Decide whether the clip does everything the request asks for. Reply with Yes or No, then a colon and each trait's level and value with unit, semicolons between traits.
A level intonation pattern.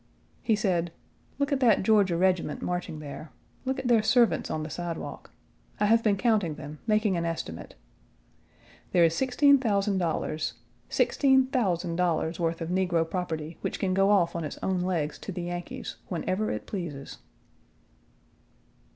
No: average, 4.4 semitones